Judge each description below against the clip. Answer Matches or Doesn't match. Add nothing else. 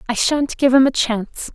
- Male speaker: Doesn't match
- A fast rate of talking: Matches